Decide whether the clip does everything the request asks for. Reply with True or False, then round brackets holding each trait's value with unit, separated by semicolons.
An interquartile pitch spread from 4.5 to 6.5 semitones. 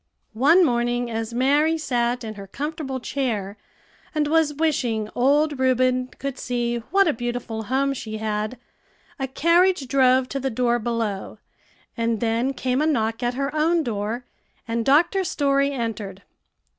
False (3.6 semitones)